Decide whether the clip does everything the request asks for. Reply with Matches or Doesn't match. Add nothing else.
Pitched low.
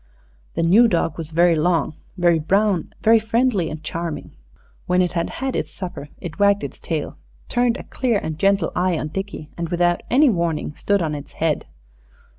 Doesn't match